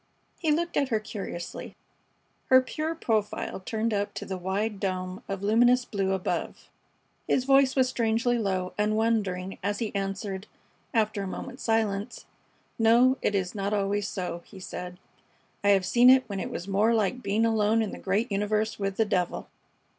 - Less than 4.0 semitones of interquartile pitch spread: Yes, average, 2.9 semitones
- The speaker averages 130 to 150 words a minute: No, average, 175 wpm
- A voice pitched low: No, high, 210 Hz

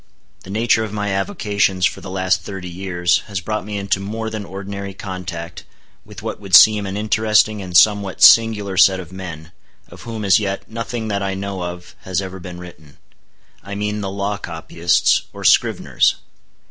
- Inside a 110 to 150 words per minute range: No, average, 175 wpm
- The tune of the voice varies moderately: No, narrow, 2.2 semitones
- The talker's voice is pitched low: Yes, low, 100 Hz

